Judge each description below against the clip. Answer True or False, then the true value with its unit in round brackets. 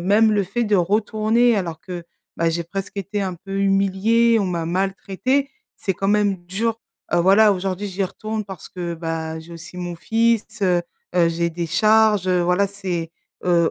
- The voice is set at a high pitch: True (195 Hz)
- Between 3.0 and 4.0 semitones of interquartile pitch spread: True (3.5 semitones)